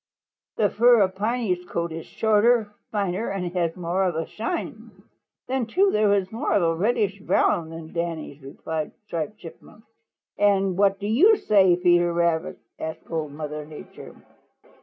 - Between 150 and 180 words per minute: Yes, average, 160 wpm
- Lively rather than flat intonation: No, average, 4.2 semitones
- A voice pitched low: No, medium, 185 Hz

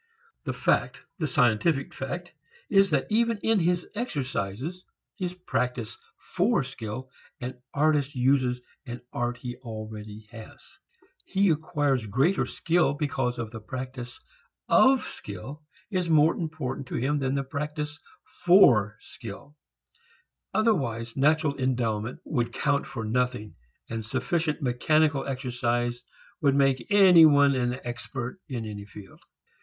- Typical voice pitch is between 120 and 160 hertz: Yes, low, 135 Hz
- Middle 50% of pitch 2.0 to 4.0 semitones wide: No, average, 4.7 semitones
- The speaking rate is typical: No, slow, 120 wpm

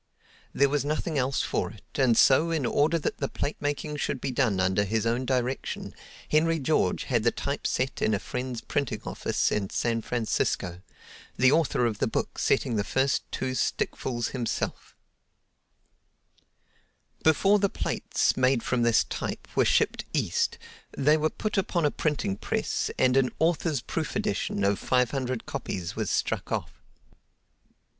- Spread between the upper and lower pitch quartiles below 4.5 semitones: Yes, average, 3.9 semitones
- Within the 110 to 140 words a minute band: No, average, 160 wpm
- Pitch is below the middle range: Yes, low, 130 Hz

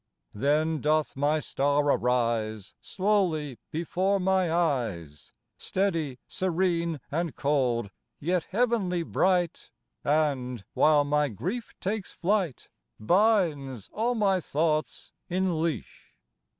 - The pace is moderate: No, slow, 100 wpm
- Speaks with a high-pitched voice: No, medium, 155 Hz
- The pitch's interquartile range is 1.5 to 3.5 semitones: No, average, 5.1 semitones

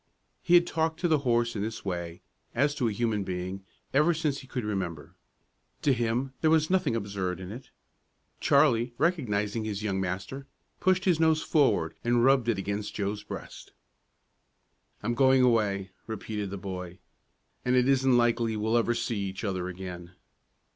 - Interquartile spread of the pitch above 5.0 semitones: Yes, wide, 5.4 semitones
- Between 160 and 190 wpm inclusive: Yes, average, 170 wpm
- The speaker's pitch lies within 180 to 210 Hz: No, low, 115 Hz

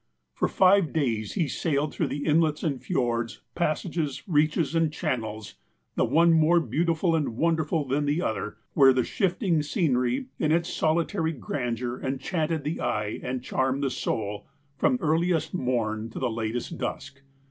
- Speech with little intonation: No, average, 4.8 semitones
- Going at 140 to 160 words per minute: Yes, average, 150 wpm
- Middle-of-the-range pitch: Yes, medium, 150 Hz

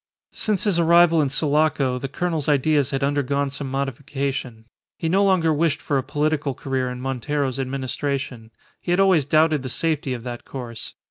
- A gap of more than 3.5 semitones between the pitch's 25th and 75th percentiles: No, average, 3.1 semitones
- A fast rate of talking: No, average, 175 wpm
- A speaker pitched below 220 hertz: Yes, medium, 140 Hz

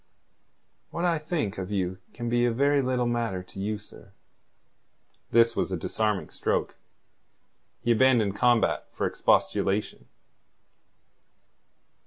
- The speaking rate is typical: No, slow, 120 wpm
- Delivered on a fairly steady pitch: No, average, 3.8 semitones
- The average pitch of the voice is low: Yes, low, 115 Hz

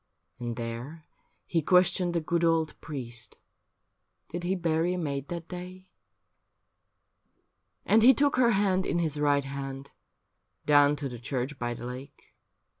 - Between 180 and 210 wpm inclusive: No, average, 145 wpm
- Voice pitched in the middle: Yes, medium, 155 Hz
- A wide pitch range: No, average, 4.6 semitones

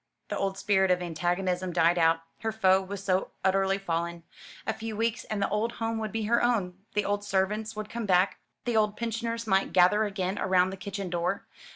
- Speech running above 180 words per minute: Yes, fast, 205 wpm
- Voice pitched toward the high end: Yes, high, 195 Hz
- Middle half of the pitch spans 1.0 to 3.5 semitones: Yes, average, 2.9 semitones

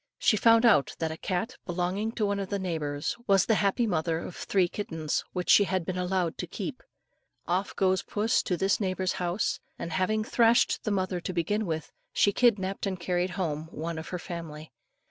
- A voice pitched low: No, medium, 185 Hz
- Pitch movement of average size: Yes, average, 3.2 semitones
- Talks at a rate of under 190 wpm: No, average, 200 wpm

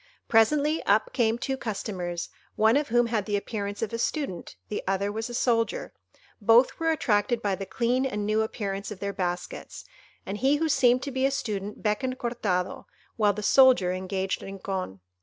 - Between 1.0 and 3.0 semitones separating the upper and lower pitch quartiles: No, average, 3.9 semitones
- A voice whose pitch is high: Yes, high, 220 Hz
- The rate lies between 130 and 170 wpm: No, average, 180 wpm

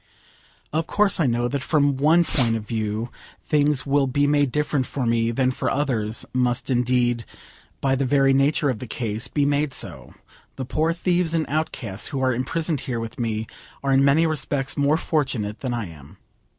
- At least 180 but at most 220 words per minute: Yes, average, 190 wpm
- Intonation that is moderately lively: Yes, average, 3.6 semitones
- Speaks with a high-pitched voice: No, low, 135 Hz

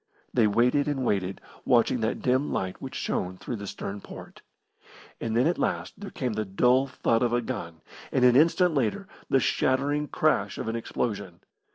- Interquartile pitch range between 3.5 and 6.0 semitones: Yes, average, 4.7 semitones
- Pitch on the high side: No, low, 120 Hz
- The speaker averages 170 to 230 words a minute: Yes, average, 185 wpm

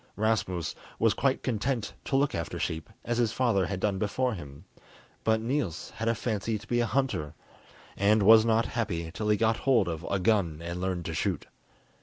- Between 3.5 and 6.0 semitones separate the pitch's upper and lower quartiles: Yes, average, 4.2 semitones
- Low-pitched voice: Yes, low, 110 Hz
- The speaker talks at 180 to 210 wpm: Yes, average, 195 wpm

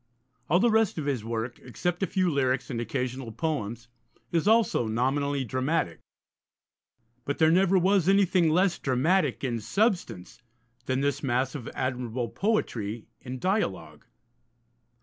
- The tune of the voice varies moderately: No, wide, 6.7 semitones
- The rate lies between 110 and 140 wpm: Yes, slow, 135 wpm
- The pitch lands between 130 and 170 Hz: Yes, medium, 140 Hz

